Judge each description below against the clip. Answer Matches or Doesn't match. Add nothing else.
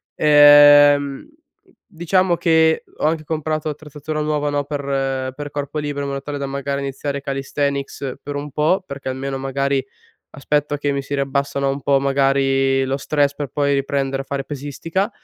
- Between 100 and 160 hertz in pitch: Matches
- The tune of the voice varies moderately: Doesn't match